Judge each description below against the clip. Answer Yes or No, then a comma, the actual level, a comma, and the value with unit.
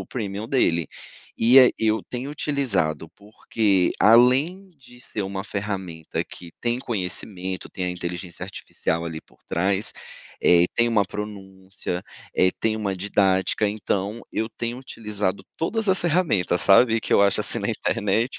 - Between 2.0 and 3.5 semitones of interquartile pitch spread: No, average, 4.1 semitones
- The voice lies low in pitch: Yes, low, 105 Hz